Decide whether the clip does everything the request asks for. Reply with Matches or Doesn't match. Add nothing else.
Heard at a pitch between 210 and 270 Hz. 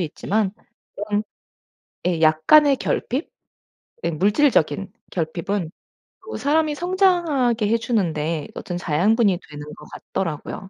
Doesn't match